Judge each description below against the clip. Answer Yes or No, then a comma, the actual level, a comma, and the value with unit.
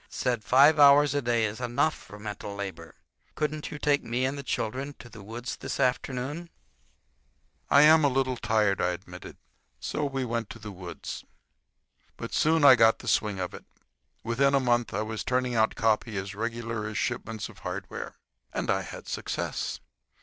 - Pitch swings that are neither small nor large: Yes, average, 4.4 semitones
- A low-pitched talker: Yes, low, 120 Hz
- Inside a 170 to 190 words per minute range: Yes, average, 180 wpm